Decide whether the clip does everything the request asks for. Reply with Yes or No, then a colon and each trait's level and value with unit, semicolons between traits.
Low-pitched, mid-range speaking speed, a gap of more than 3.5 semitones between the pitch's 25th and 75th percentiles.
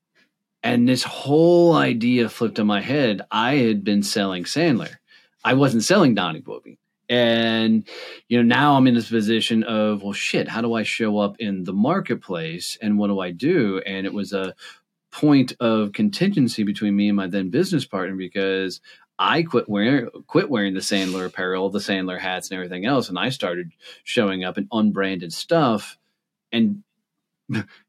Yes: low, 105 Hz; average, 170 wpm; average, 4.3 semitones